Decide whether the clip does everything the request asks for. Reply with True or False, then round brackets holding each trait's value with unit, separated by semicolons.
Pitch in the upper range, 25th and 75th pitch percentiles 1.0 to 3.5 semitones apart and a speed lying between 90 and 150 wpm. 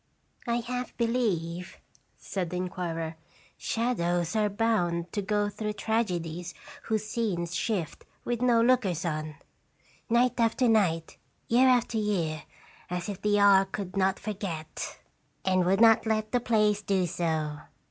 False (200 Hz; 4.5 semitones; 140 wpm)